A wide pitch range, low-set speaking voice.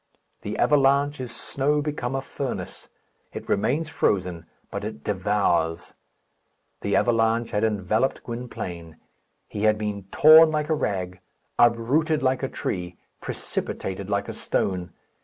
Yes: wide, 6.0 semitones; low, 115 Hz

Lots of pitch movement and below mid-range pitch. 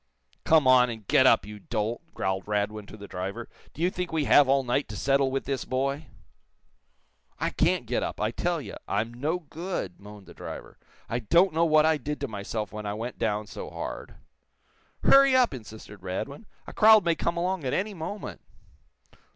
Yes: wide, 7.2 semitones; low, 130 Hz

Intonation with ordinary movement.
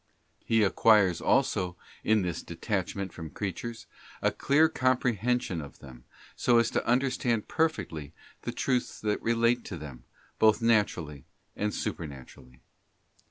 No: wide, 6.3 semitones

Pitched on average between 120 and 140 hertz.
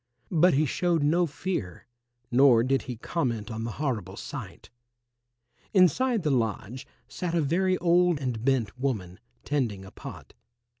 Yes: low, 135 Hz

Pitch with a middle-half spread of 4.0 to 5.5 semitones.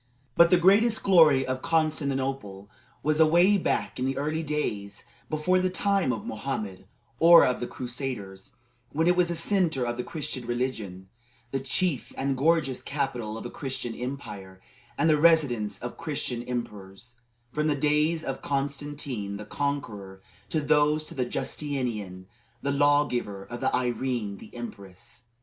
Yes: average, 4.5 semitones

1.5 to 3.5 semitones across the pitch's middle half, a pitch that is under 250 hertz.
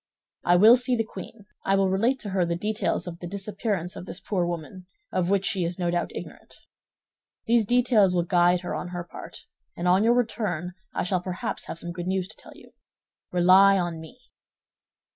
Yes: average, 3.1 semitones; medium, 185 Hz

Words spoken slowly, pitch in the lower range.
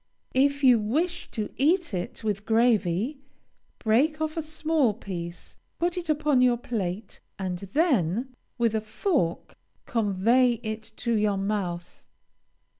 No: slow, 130 wpm; high, 230 Hz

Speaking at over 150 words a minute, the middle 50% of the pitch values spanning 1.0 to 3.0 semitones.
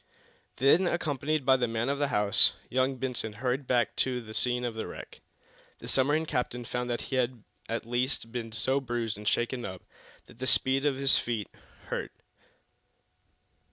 Yes: average, 170 wpm; narrow, 2.4 semitones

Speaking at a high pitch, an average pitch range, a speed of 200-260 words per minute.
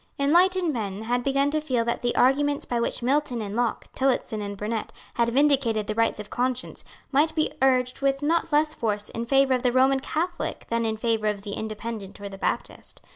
Yes: high, 245 Hz; average, 4.2 semitones; fast, 205 wpm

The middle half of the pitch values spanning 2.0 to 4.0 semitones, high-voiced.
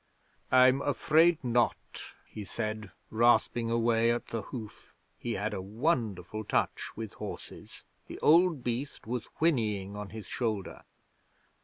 No: average, 3.1 semitones; low, 115 Hz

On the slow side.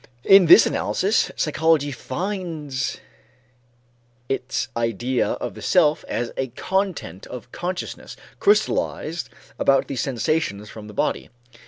Yes: slow, 115 wpm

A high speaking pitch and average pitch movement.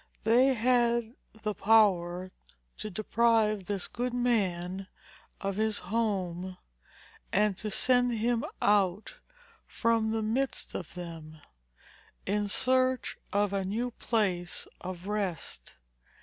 Yes: high, 210 Hz; average, 3.7 semitones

